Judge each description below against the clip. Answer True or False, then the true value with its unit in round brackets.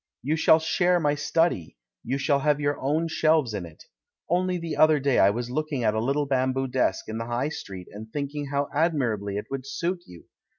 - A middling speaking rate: False (220 wpm)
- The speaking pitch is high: False (140 Hz)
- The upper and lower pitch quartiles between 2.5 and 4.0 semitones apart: False (5.2 semitones)